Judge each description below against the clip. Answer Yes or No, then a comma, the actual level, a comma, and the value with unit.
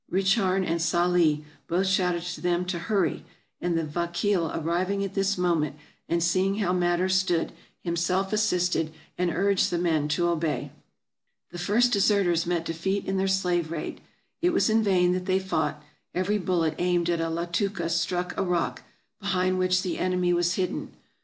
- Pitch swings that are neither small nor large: No, narrow, 2.0 semitones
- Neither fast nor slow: Yes, average, 180 wpm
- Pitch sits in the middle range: Yes, medium, 180 Hz